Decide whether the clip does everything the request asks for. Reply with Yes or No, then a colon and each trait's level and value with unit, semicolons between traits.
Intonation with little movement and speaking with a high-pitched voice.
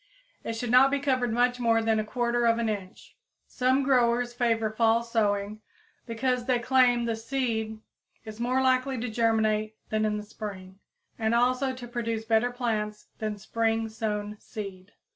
Yes: narrow, 2.2 semitones; high, 230 Hz